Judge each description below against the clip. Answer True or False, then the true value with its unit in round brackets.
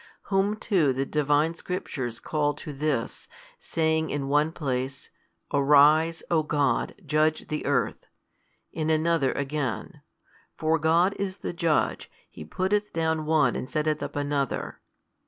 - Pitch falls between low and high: True (155 Hz)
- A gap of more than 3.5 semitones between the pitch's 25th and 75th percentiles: False (2.4 semitones)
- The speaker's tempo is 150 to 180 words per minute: False (135 wpm)